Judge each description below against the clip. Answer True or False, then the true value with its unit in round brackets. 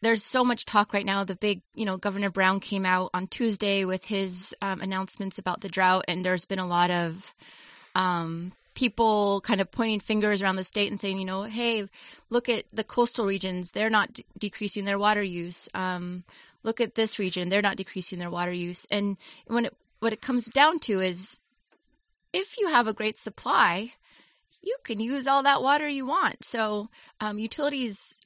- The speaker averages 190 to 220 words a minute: True (195 wpm)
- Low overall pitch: False (205 Hz)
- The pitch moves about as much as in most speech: True (3.5 semitones)